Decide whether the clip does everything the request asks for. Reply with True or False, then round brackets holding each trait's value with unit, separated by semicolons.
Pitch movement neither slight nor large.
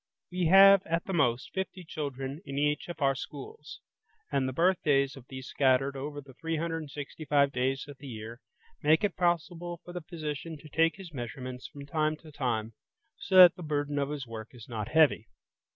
True (3.8 semitones)